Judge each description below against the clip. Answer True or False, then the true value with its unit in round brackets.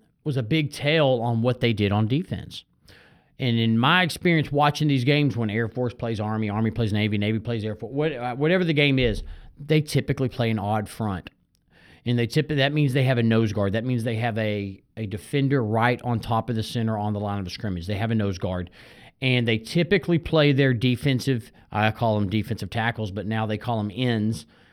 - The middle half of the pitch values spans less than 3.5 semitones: False (4.0 semitones)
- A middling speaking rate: False (220 wpm)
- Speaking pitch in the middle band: False (120 Hz)